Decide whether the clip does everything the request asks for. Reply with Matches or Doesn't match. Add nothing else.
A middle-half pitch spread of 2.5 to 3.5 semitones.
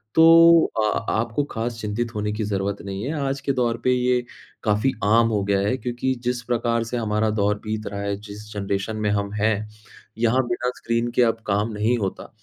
Matches